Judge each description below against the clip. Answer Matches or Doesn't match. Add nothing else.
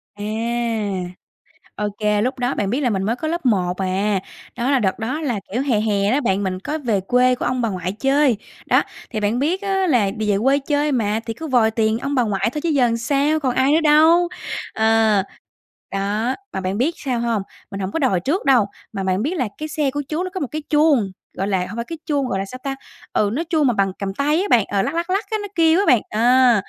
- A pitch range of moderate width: Doesn't match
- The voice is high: Matches